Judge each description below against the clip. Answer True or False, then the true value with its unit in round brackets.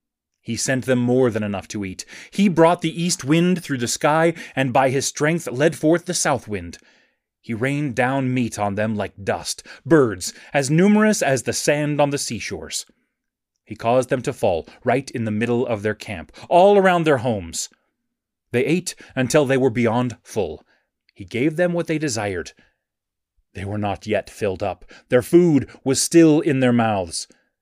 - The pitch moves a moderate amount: False (5.9 semitones)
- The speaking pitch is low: True (130 Hz)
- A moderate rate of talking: True (180 wpm)